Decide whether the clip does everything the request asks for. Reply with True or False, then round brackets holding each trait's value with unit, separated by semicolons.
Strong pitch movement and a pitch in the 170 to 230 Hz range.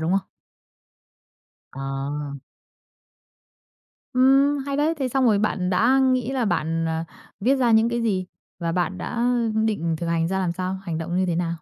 True (6.9 semitones; 190 Hz)